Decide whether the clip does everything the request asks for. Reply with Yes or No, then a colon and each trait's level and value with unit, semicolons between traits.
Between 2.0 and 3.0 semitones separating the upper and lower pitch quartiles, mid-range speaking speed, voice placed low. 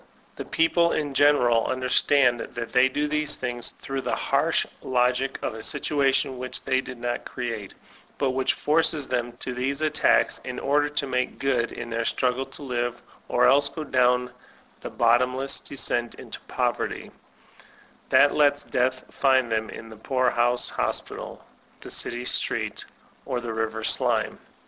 Yes: narrow, 2.4 semitones; average, 155 wpm; low, 130 Hz